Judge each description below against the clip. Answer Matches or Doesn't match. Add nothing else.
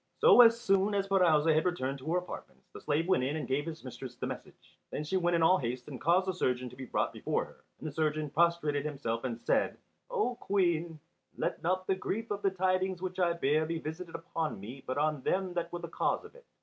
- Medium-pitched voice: Matches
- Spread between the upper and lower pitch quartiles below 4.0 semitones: Doesn't match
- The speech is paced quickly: Matches